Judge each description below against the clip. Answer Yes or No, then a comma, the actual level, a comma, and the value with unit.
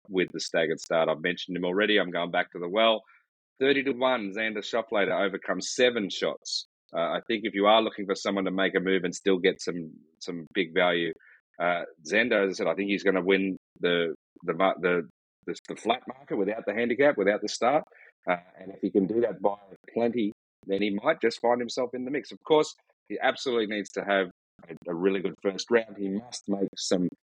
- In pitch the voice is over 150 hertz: No, low, 100 Hz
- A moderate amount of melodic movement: Yes, average, 3.5 semitones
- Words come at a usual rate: No, fast, 225 wpm